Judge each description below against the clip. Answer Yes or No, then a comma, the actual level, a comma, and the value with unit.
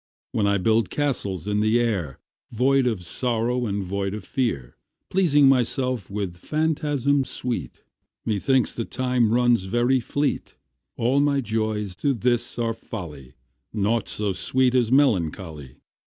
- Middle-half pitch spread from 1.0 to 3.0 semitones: No, average, 4.4 semitones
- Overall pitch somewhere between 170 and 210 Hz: No, low, 115 Hz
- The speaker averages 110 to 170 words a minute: Yes, average, 140 wpm